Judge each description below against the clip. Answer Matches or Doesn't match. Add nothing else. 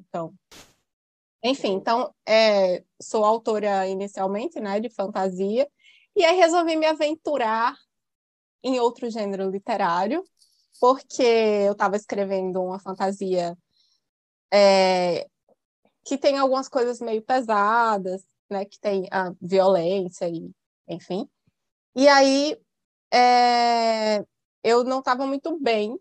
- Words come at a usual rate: Doesn't match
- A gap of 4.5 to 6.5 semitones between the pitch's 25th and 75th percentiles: Matches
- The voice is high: Matches